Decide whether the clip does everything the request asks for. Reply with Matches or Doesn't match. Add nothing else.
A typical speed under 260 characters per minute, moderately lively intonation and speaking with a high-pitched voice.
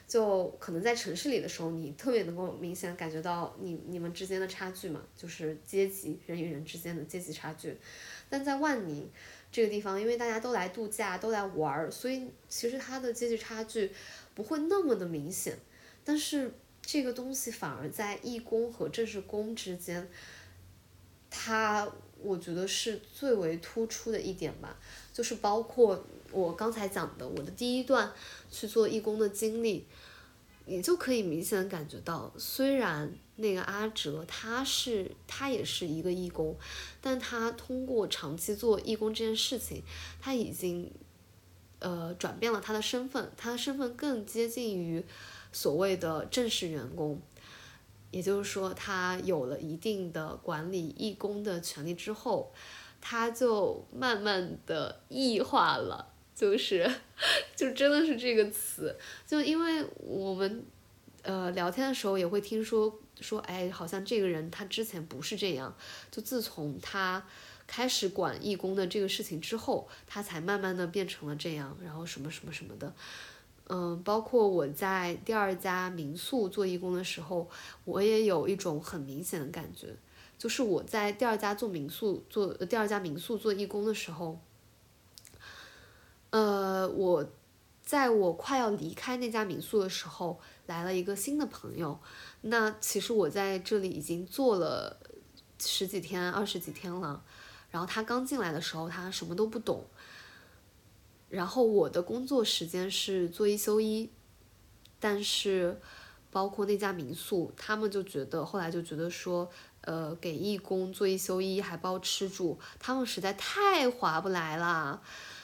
Matches